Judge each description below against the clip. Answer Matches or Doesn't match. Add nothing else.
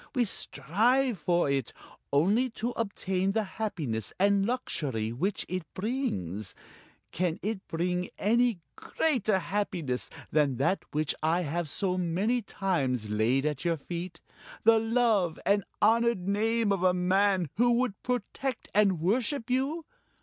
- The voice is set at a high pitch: Matches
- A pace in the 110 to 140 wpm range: Matches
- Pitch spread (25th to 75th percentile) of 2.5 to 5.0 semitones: Doesn't match